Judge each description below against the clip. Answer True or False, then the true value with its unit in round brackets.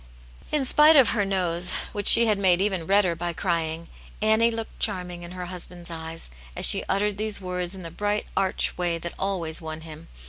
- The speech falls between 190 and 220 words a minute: True (205 wpm)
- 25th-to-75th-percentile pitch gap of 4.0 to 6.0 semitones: False (3.4 semitones)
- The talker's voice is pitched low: False (180 Hz)